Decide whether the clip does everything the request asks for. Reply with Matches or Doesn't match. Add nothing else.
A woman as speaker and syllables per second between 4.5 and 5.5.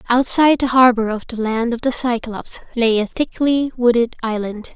Matches